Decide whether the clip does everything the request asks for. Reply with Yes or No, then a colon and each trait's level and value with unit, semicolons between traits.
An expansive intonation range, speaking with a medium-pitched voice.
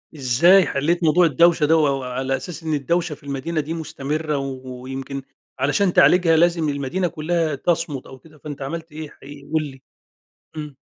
No: average, 3.4 semitones; medium, 150 Hz